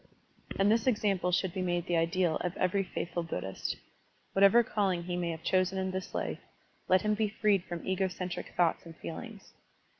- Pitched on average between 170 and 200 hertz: Yes, medium, 185 Hz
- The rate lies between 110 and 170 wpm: No, average, 185 wpm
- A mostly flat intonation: Yes, narrow, 2.3 semitones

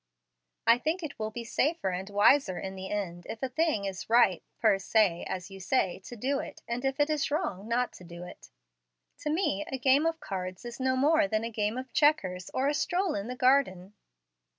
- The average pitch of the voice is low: No, high, 230 Hz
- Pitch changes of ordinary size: No, wide, 6.4 semitones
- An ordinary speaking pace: No, fast, 210 wpm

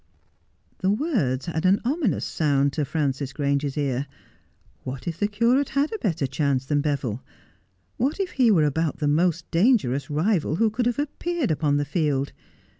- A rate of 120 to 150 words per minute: No, average, 170 wpm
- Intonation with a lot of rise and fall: Yes, wide, 7.8 semitones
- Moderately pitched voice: Yes, medium, 160 Hz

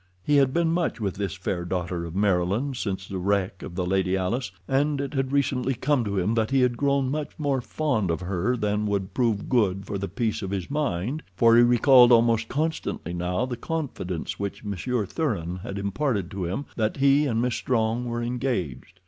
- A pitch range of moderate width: No, wide, 5.7 semitones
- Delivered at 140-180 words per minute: No, fast, 205 wpm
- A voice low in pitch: Yes, low, 115 Hz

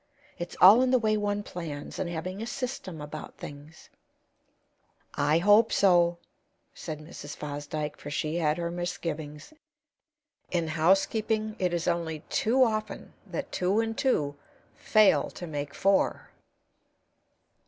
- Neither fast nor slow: No, slow, 130 wpm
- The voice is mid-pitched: Yes, medium, 175 Hz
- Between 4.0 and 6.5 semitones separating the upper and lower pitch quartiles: Yes, average, 5.3 semitones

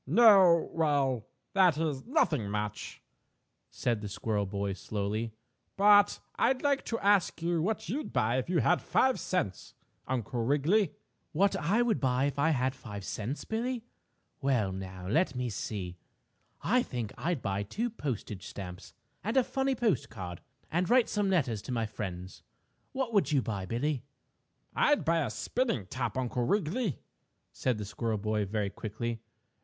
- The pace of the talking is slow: No, average, 160 wpm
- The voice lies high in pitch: No, low, 130 Hz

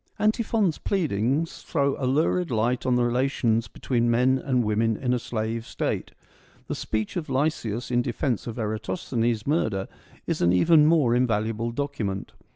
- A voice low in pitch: Yes, low, 120 Hz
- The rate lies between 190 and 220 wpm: No, average, 155 wpm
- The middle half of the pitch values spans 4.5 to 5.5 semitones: No, average, 4.1 semitones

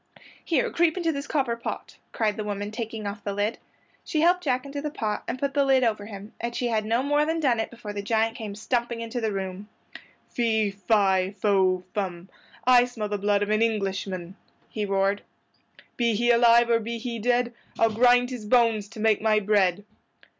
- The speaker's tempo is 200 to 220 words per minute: Yes, fast, 205 wpm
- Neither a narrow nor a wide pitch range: Yes, average, 3.1 semitones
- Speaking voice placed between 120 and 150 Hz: No, high, 225 Hz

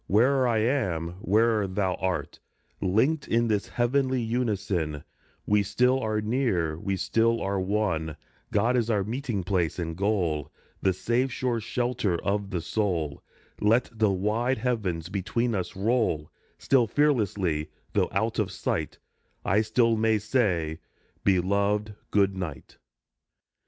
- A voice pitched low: Yes, low, 105 Hz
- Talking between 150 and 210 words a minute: No, slow, 135 wpm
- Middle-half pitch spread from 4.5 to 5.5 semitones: No, average, 4.1 semitones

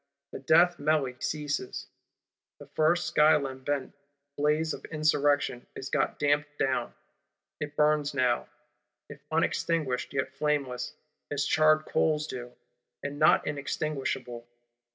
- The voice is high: No, medium, 145 Hz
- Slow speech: Yes, slow, 115 wpm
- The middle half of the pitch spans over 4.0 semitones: No, narrow, 2.5 semitones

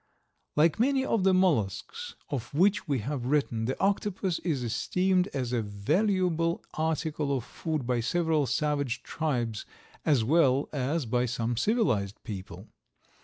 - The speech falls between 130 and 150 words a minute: Yes, average, 140 wpm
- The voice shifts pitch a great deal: Yes, wide, 6.7 semitones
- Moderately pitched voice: Yes, medium, 150 Hz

